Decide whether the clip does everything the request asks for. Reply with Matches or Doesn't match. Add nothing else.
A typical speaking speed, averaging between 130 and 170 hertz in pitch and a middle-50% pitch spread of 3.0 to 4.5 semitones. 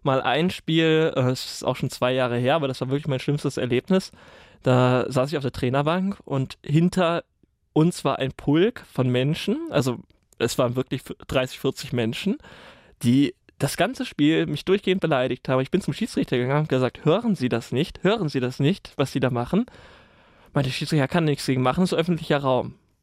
Doesn't match